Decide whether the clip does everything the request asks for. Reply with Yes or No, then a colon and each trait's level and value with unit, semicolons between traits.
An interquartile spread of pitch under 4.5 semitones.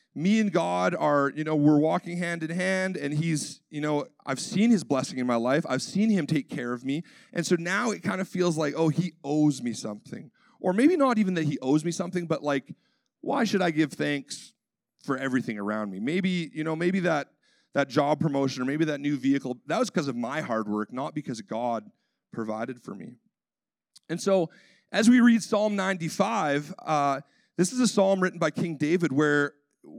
No: average, 4.8 semitones